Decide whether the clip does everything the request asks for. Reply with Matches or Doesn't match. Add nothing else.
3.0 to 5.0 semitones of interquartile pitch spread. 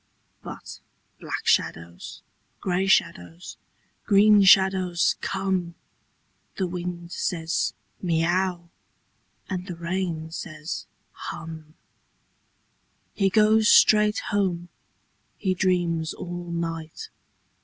Doesn't match